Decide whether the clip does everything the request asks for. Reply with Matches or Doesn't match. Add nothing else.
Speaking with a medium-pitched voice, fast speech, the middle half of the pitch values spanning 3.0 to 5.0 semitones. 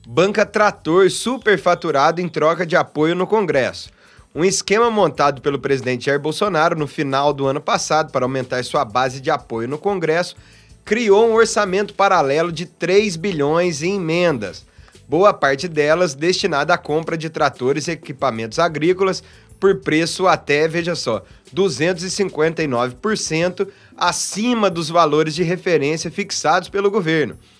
Doesn't match